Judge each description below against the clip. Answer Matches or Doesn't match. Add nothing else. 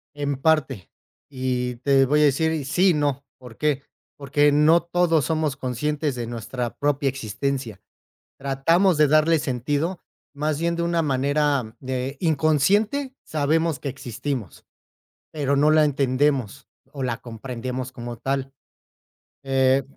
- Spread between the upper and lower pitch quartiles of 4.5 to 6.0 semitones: Doesn't match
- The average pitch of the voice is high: Doesn't match